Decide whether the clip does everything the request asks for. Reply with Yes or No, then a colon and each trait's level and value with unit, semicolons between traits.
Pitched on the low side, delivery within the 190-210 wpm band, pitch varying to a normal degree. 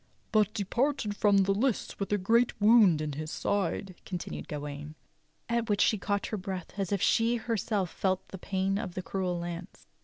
No: high, 195 Hz; average, 195 wpm; average, 3.0 semitones